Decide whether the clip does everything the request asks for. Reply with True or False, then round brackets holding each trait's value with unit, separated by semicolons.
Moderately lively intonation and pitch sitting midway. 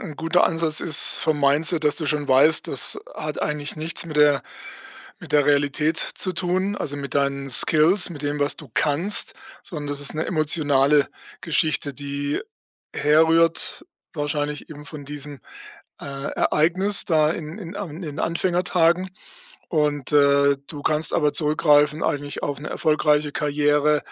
False (2.1 semitones; 150 Hz)